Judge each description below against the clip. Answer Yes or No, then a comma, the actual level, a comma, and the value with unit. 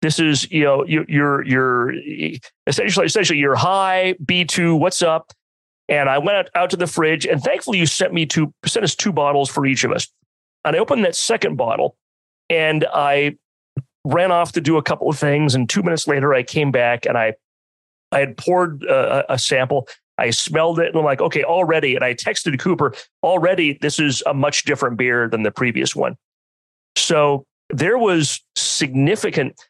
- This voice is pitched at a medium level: Yes, medium, 145 Hz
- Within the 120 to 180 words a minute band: No, average, 190 wpm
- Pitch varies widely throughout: No, average, 4.3 semitones